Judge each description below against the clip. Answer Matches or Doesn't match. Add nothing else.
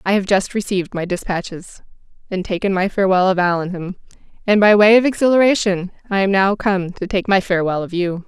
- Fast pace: Doesn't match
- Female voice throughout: Matches